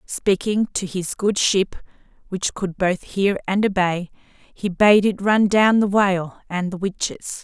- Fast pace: No, average, 170 wpm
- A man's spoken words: No, female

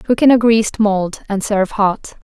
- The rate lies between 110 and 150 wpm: No, fast, 210 wpm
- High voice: Yes, high, 210 Hz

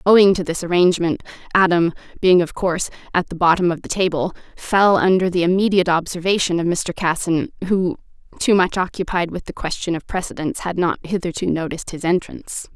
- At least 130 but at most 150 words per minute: No, average, 175 wpm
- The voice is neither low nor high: Yes, medium, 175 Hz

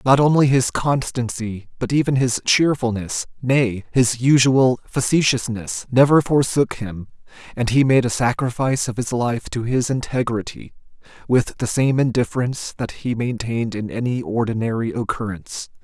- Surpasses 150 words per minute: No, average, 140 wpm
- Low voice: Yes, low, 125 Hz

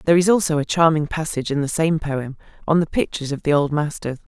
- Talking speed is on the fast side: Yes, fast, 235 wpm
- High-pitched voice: No, medium, 155 Hz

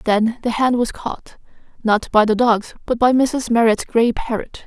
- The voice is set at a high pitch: Yes, high, 230 Hz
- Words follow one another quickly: No, average, 195 wpm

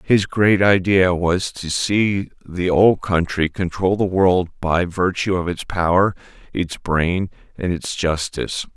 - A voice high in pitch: No, very low, 90 Hz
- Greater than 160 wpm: No, average, 150 wpm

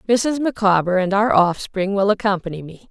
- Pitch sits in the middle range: No, high, 200 Hz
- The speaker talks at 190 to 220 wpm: No, average, 165 wpm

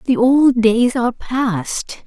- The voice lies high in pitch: Yes, high, 235 Hz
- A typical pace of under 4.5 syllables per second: Yes, 3.8 syllables/s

